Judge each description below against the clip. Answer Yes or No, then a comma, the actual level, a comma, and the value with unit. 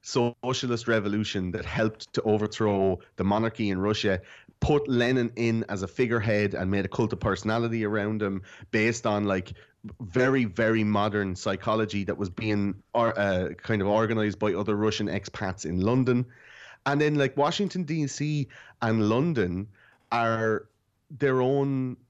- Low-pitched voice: Yes, low, 110 Hz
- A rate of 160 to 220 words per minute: No, average, 145 wpm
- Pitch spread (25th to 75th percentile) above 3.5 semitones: No, average, 3.2 semitones